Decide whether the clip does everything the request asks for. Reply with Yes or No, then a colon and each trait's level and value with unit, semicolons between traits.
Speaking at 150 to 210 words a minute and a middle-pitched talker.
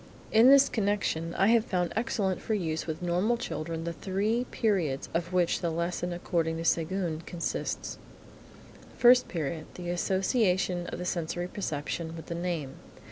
Yes: average, 155 wpm; medium, 175 Hz